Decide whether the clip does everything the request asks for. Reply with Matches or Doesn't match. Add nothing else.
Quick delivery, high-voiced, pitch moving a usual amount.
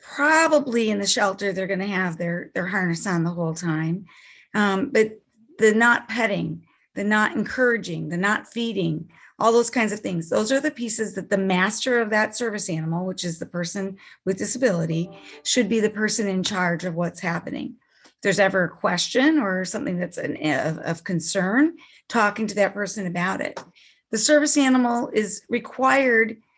Doesn't match